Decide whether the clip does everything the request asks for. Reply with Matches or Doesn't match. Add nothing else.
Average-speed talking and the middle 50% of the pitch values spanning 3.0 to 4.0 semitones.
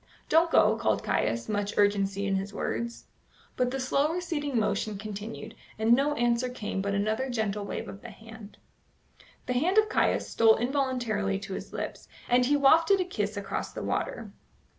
Doesn't match